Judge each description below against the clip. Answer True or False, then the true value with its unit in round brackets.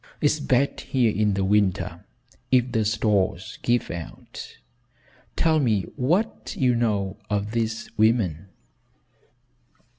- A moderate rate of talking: False (115 wpm)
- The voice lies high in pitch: False (110 Hz)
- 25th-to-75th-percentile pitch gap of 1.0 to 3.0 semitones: False (3.6 semitones)